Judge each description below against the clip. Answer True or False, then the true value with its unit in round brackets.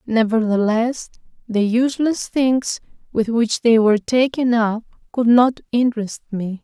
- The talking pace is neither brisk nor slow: False (125 wpm)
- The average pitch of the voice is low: False (230 Hz)